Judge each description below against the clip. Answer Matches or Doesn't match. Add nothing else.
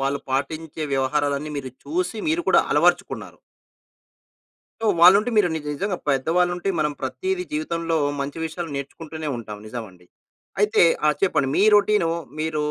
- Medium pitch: Matches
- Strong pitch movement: Matches